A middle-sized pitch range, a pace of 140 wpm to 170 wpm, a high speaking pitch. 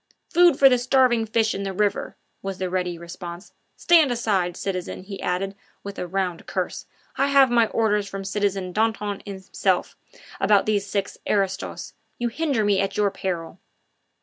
Yes: average, 3.1 semitones; average, 165 wpm; high, 200 Hz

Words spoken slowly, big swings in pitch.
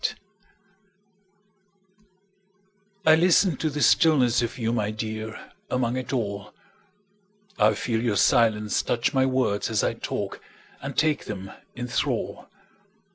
Yes: slow, 115 wpm; wide, 6.2 semitones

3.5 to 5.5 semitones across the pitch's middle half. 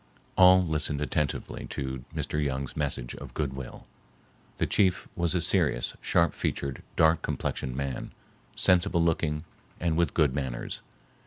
Yes: average, 4.0 semitones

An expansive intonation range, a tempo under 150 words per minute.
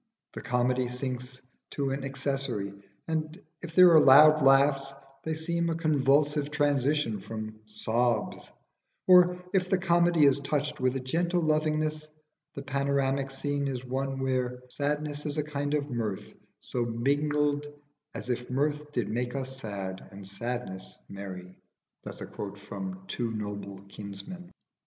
No: average, 3.8 semitones; average, 140 wpm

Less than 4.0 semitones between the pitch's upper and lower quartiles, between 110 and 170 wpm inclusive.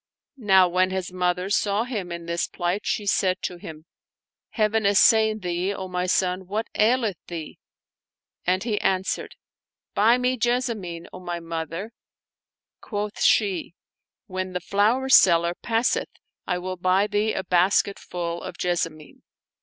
Yes: average, 3.2 semitones; average, 150 wpm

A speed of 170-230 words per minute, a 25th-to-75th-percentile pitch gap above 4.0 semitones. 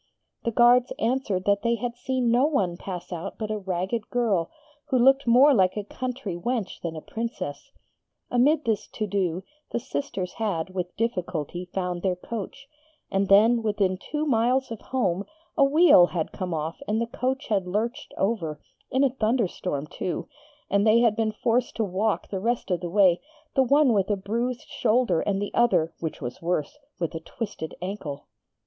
Yes: average, 180 wpm; average, 5.0 semitones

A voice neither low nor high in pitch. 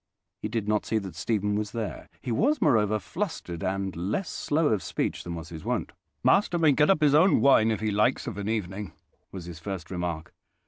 No: low, 105 Hz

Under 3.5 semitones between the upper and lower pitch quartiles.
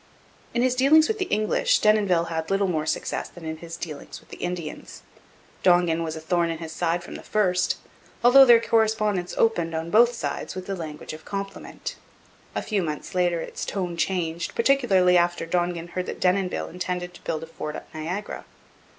No: average, 3.9 semitones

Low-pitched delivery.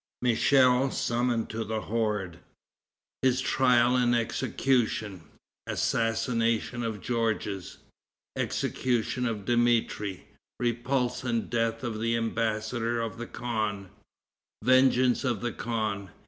Yes: low, 115 Hz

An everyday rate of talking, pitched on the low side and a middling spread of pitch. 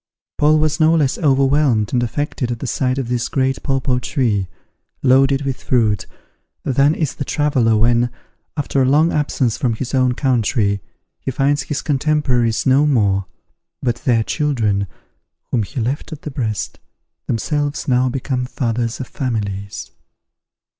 Yes: average, 155 wpm; low, 130 Hz; average, 3.5 semitones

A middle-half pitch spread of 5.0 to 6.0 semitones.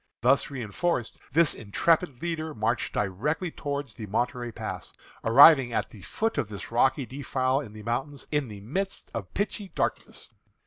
Yes: average, 5.3 semitones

